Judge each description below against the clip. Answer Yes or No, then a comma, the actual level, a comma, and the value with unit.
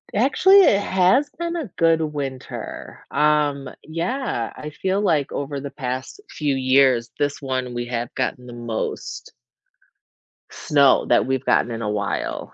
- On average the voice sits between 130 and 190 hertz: Yes, medium, 140 Hz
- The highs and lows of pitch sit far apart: No, average, 4.9 semitones